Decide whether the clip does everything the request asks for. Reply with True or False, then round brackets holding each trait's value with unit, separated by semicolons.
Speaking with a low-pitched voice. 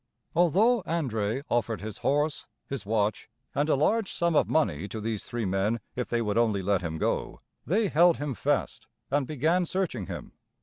True (125 Hz)